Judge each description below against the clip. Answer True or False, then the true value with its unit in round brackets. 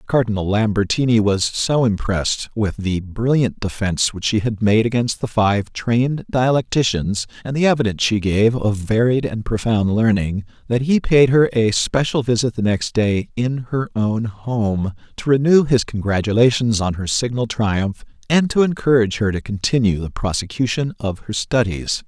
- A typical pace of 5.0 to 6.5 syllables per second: False (4.8 syllables/s)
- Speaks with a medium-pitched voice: False (115 Hz)